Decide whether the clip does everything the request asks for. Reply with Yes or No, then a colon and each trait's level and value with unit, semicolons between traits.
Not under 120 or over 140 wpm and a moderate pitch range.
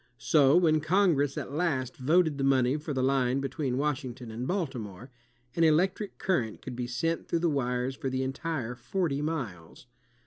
No: average, 170 wpm; average, 4.3 semitones